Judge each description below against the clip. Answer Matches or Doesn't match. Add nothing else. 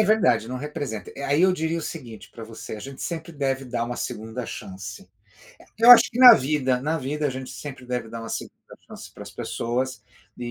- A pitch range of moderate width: Matches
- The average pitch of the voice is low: Matches